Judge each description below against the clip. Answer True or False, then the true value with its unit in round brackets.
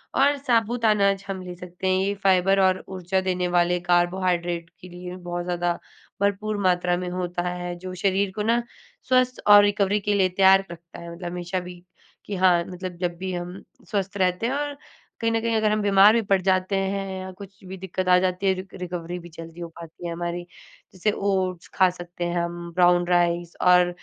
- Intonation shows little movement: True (1.9 semitones)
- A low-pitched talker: False (185 Hz)